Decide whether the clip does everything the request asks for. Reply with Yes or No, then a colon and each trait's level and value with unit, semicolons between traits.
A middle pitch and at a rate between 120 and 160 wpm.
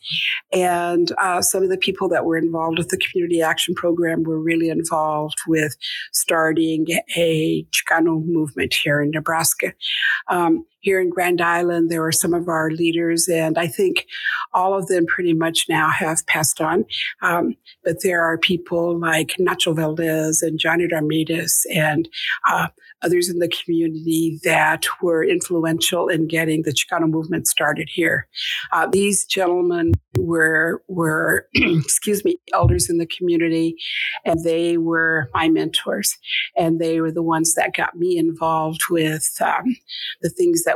Yes: medium, 165 Hz; average, 155 wpm